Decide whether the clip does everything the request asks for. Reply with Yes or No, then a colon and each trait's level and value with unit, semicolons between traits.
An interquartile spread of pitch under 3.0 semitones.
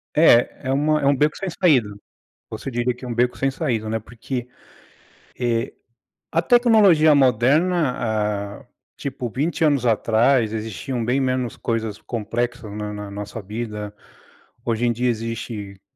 No: average, 4.0 semitones